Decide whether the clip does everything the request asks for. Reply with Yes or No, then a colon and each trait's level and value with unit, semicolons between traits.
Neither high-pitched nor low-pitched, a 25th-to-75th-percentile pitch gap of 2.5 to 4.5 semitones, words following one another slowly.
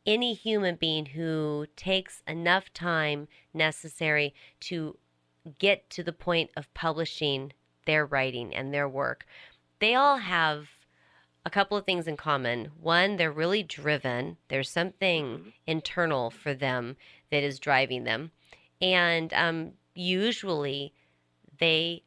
Yes: medium, 160 Hz; average, 3.6 semitones; slow, 125 wpm